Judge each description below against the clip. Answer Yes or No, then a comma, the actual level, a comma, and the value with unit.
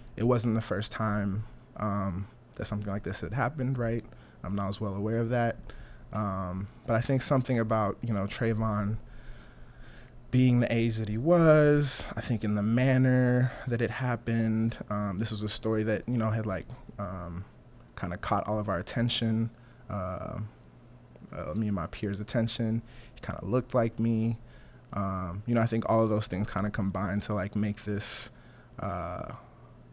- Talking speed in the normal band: Yes, average, 180 wpm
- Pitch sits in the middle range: No, low, 110 Hz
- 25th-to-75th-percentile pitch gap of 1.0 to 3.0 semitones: Yes, narrow, 2.6 semitones